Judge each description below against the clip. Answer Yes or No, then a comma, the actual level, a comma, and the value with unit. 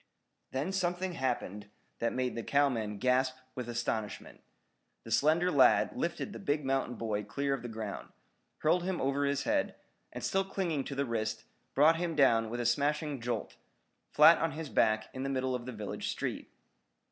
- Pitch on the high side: No, low, 135 Hz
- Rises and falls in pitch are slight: No, average, 4.5 semitones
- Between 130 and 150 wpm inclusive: No, average, 180 wpm